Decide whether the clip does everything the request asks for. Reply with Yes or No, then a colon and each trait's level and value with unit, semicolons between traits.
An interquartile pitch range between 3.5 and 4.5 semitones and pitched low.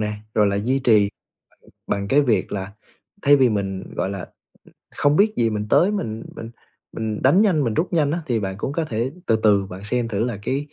No: wide, 5.5 semitones; low, 115 Hz